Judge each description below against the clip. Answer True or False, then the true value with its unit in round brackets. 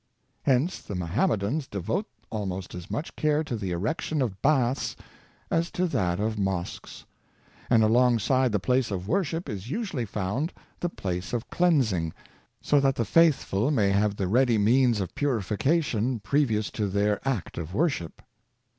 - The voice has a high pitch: False (115 Hz)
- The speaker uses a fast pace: False (160 wpm)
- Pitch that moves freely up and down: True (6.2 semitones)